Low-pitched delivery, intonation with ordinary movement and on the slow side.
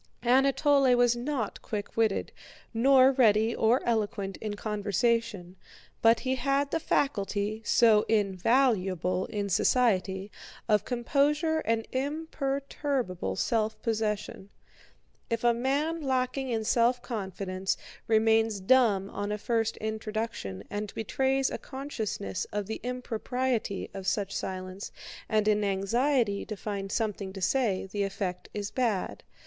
No: high, 220 Hz; average, 4.1 semitones; slow, 125 wpm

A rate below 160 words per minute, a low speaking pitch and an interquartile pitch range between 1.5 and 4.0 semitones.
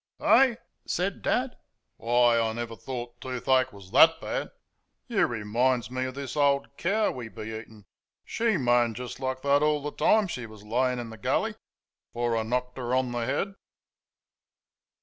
No: average, 170 wpm; low, 125 Hz; average, 3.2 semitones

